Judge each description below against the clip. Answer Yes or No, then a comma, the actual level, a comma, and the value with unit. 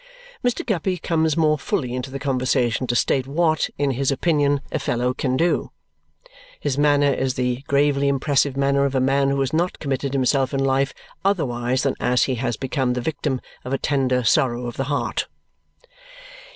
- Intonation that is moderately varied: No, narrow, 2.1 semitones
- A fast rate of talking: No, average, 180 wpm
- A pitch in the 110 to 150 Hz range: Yes, low, 135 Hz